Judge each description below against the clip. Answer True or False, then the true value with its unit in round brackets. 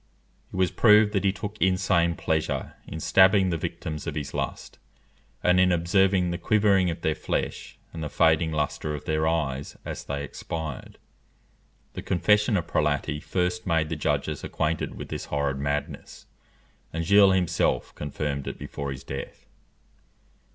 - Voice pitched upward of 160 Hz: False (85 Hz)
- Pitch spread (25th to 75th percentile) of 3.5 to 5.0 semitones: True (3.8 semitones)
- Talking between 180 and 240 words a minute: False (160 wpm)